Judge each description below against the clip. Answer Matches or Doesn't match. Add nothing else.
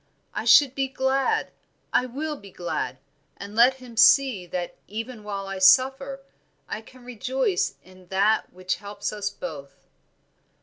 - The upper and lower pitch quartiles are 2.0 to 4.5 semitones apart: Doesn't match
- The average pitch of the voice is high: Matches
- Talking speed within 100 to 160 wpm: Matches